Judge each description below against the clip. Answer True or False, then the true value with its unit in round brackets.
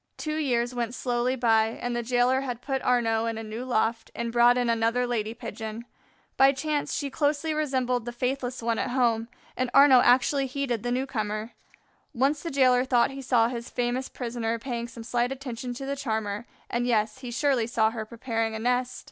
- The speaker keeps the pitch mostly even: True (2.3 semitones)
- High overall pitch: True (245 Hz)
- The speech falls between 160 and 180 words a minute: False (190 wpm)